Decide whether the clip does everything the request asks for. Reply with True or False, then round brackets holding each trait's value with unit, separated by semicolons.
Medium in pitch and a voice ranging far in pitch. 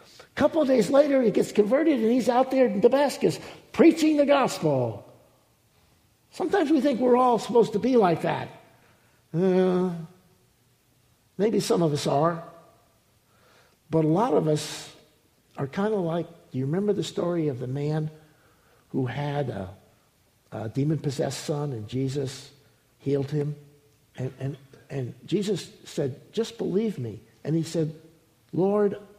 True (160 Hz; 7.2 semitones)